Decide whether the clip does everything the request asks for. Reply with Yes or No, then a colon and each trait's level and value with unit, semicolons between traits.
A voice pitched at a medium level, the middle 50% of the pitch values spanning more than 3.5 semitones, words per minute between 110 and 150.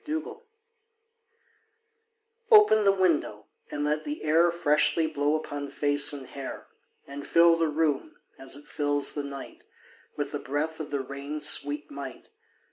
No: medium, 145 Hz; narrow, 2.4 semitones; average, 145 wpm